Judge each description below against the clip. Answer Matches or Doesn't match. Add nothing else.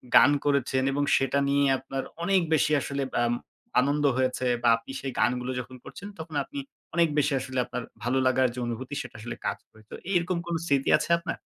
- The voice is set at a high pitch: Doesn't match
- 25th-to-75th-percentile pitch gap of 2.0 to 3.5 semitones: Matches